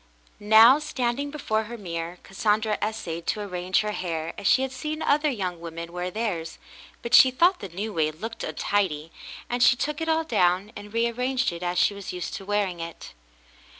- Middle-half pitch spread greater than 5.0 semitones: Yes, wide, 5.5 semitones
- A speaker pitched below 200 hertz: No, high, 210 Hz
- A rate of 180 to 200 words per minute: Yes, average, 190 wpm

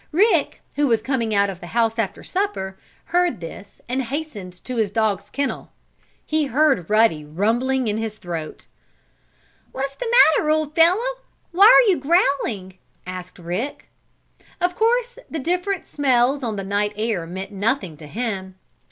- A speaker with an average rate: Yes, average, 155 wpm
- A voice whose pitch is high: Yes, high, 235 Hz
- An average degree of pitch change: No, wide, 7.9 semitones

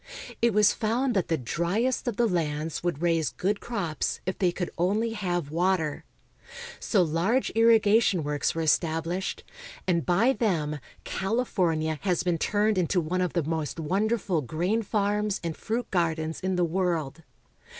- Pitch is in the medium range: Yes, medium, 180 Hz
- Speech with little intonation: No, average, 4.4 semitones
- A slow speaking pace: No, average, 160 wpm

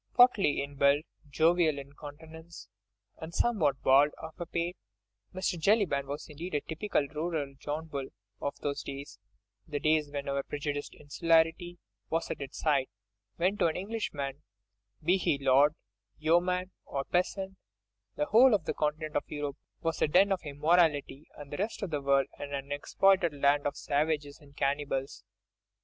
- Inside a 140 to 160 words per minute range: Yes, average, 155 wpm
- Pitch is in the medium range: Yes, medium, 150 Hz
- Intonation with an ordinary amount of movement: Yes, average, 3.3 semitones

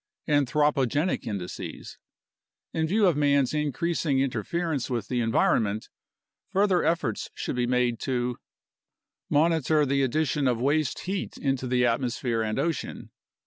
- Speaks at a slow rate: Yes, slow, 125 wpm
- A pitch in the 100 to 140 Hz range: Yes, low, 135 Hz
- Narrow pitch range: No, average, 4.3 semitones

